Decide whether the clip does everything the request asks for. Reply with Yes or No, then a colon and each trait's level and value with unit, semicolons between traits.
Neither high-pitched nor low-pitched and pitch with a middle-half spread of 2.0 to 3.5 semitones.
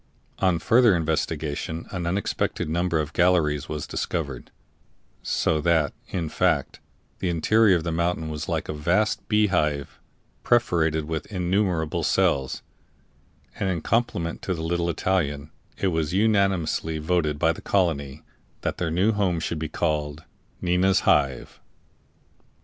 No: very low, 85 Hz; average, 3.1 semitones